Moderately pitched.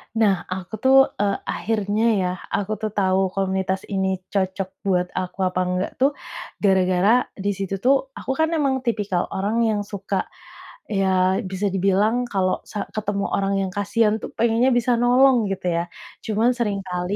No: high, 200 Hz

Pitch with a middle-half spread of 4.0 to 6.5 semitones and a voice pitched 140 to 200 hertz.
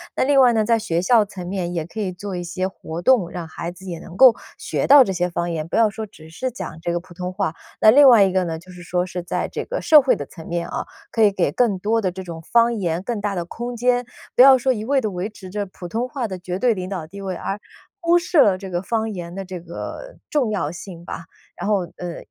Yes: average, 4.6 semitones; high, 190 Hz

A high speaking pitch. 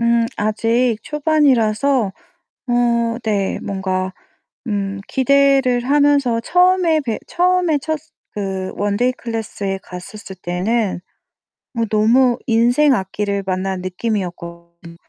Yes: high, 225 Hz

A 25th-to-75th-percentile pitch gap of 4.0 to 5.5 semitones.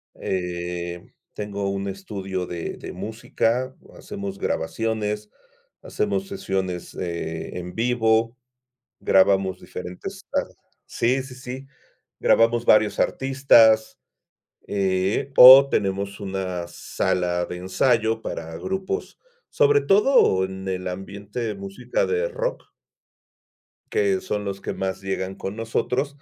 Yes: average, 4.3 semitones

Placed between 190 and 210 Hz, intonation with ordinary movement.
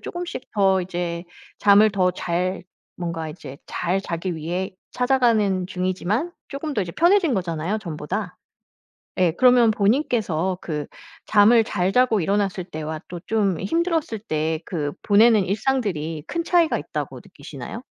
Yes: high, 195 Hz; average, 4.9 semitones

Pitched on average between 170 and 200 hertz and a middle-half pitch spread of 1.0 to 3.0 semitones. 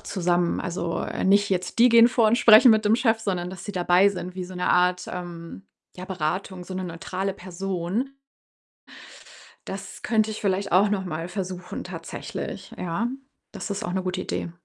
Yes: high, 190 Hz; narrow, 2.5 semitones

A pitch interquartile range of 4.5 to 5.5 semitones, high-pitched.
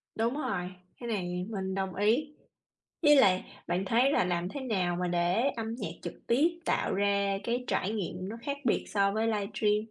No: average, 4.1 semitones; high, 205 Hz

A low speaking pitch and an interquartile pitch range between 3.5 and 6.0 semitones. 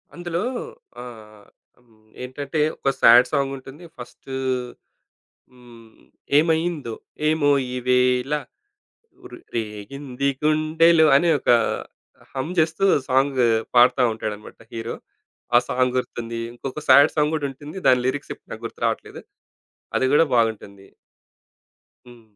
Yes: low, 130 Hz; average, 4.1 semitones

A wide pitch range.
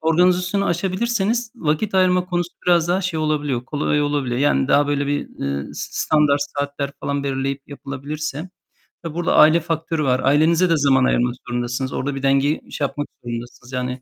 No: average, 3.8 semitones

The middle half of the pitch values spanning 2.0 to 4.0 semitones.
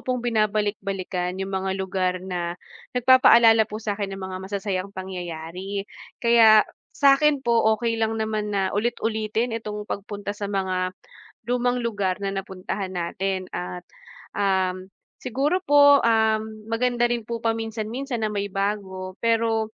Yes: average, 3.3 semitones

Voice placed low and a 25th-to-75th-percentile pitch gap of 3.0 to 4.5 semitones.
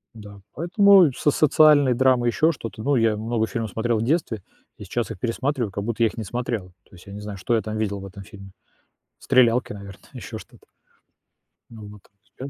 Yes: low, 115 Hz; average, 3.9 semitones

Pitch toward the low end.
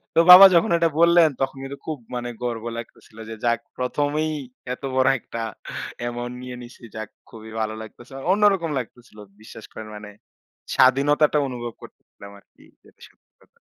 Yes: low, 125 Hz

